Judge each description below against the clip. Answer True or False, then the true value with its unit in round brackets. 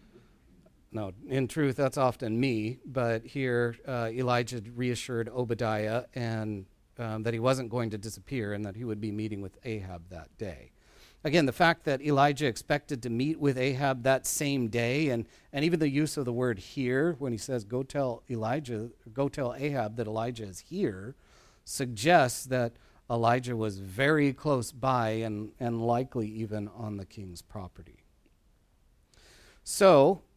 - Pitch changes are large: False (3.4 semitones)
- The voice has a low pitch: True (120 Hz)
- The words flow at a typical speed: True (160 wpm)